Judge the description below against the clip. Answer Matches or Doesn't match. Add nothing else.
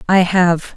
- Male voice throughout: Doesn't match